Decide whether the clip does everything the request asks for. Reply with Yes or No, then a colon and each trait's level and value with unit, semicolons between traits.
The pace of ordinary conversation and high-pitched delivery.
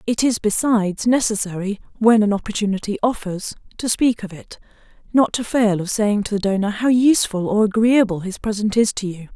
Yes: average, 185 wpm; high, 215 Hz